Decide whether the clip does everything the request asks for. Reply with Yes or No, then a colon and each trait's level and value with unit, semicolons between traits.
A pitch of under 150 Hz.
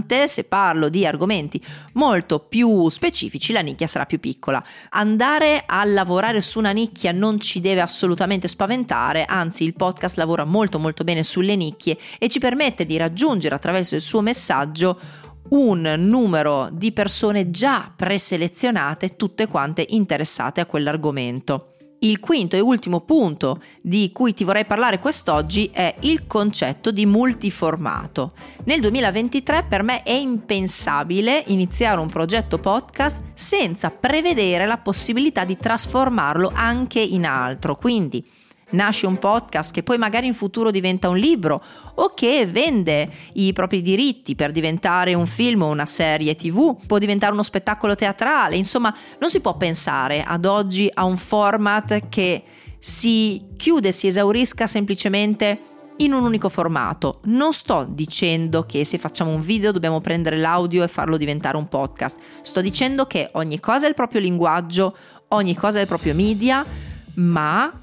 No: high, 195 Hz